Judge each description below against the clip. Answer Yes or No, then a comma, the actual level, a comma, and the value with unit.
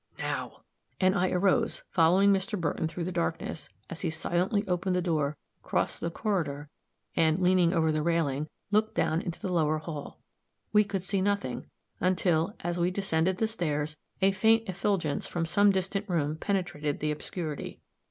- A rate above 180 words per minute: No, average, 165 wpm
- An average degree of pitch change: Yes, average, 3.3 semitones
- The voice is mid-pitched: Yes, medium, 175 Hz